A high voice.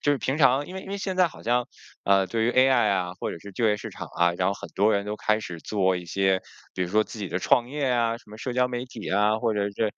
No: low, 110 Hz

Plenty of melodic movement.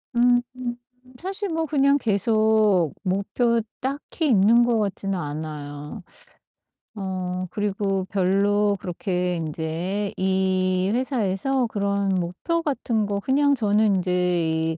No: average, 4.3 semitones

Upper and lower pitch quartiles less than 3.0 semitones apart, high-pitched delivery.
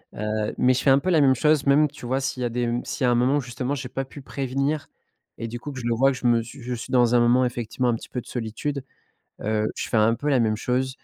No: narrow, 2.5 semitones; low, 125 Hz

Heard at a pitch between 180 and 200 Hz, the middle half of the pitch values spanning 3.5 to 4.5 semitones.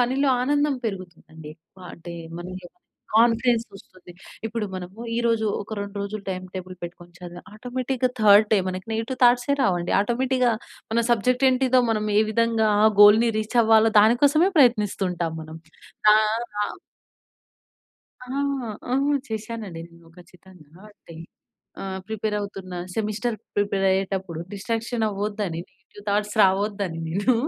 No: high, 210 Hz; average, 3.9 semitones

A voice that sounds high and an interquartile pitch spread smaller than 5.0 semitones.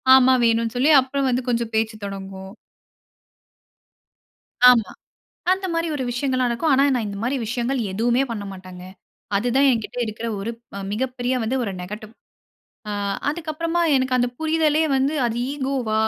Yes: high, 245 Hz; average, 3.8 semitones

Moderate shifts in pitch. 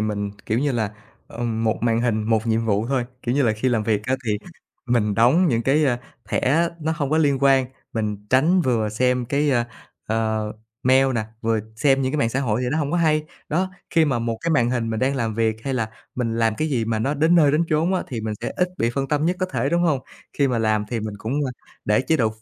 Yes: average, 4.4 semitones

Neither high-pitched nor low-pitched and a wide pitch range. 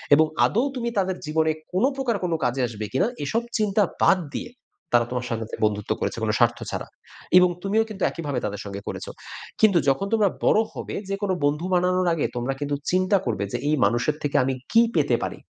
Yes: medium, 160 Hz; wide, 8.3 semitones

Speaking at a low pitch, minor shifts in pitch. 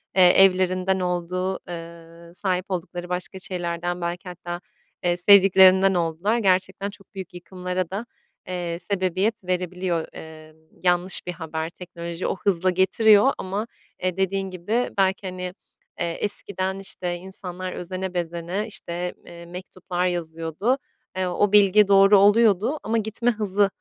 No: medium, 185 Hz; narrow, 1.9 semitones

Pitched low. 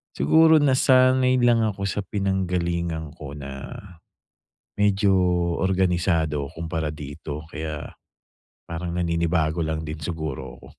Yes: very low, 85 Hz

